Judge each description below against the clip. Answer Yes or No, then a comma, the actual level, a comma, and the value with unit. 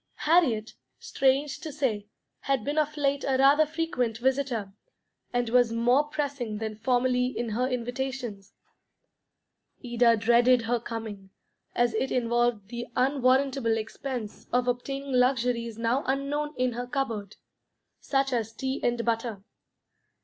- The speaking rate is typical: No, slow, 130 wpm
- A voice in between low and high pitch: No, high, 245 Hz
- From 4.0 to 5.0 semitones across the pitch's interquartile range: No, average, 2.9 semitones